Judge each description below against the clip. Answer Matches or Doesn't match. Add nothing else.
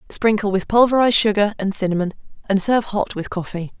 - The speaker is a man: Doesn't match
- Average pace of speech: Matches